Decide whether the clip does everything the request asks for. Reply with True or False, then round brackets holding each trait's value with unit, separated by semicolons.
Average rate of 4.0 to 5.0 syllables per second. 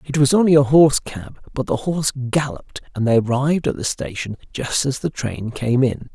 False (5.3 syllables/s)